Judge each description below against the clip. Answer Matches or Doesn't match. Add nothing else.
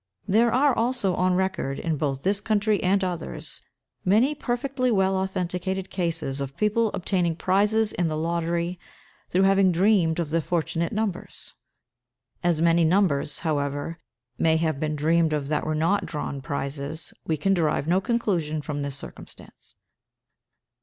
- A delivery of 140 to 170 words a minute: Matches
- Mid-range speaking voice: Matches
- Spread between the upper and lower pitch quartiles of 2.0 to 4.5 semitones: Matches